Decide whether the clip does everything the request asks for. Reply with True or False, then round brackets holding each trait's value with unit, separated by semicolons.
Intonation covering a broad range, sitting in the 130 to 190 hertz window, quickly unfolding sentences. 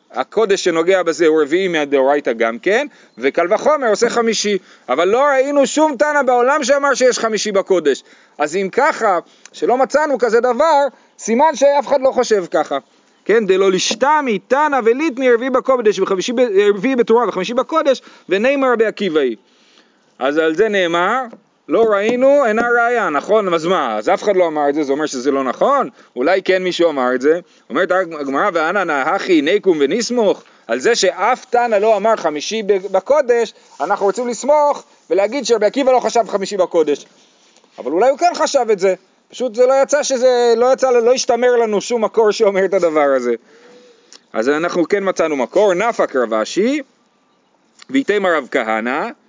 False (5.9 semitones; 225 Hz; 165 wpm)